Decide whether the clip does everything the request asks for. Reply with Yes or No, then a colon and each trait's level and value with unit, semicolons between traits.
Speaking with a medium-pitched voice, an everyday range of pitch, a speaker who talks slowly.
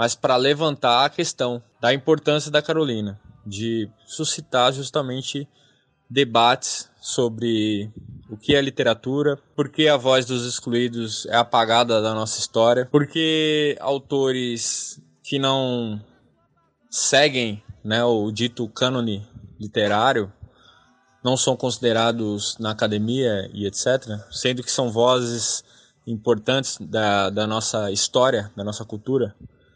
No: low, 120 Hz; average, 3.5 semitones; slow, 115 wpm